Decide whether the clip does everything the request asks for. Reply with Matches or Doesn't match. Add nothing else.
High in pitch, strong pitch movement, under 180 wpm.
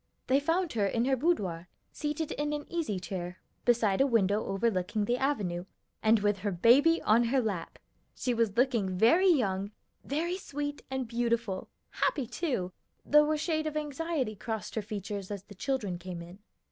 Matches